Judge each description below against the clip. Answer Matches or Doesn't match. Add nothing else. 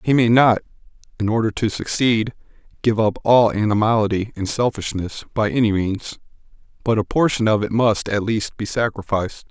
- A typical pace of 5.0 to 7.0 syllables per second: Matches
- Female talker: Doesn't match